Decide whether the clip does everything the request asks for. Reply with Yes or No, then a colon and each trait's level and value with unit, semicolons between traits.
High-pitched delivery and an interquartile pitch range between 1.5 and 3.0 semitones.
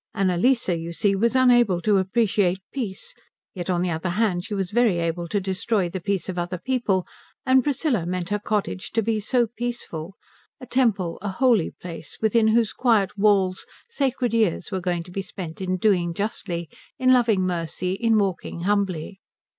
No: high, 195 Hz; average, 4.2 semitones